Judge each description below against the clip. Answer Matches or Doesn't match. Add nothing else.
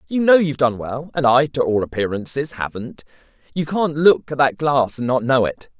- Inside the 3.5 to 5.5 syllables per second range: Matches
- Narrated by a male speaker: Matches